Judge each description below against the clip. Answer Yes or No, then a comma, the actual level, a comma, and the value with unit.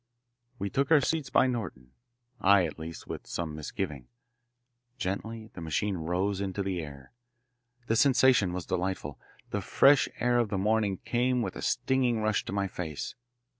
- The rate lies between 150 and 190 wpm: Yes, average, 165 wpm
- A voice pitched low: Yes, low, 100 Hz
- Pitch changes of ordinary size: No, wide, 5.7 semitones